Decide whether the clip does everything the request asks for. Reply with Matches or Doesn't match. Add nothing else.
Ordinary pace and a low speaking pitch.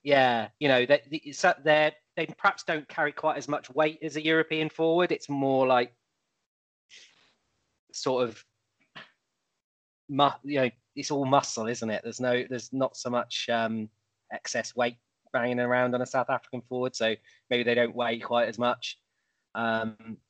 Matches